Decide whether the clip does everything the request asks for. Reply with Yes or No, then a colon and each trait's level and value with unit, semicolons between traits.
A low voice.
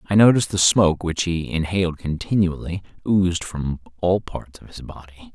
Yes: very low, 90 Hz